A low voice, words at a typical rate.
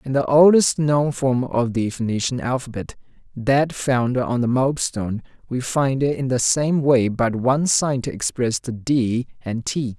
Yes: low, 130 Hz; average, 180 wpm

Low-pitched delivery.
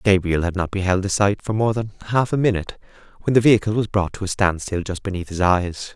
Yes: low, 100 Hz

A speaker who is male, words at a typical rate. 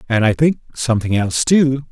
Yes: male; average, 190 wpm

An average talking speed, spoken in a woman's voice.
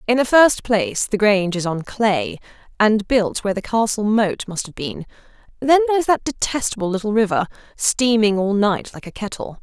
Yes: average, 185 wpm; female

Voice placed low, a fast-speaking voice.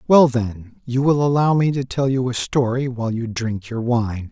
Yes: low, 125 Hz; fast, 225 wpm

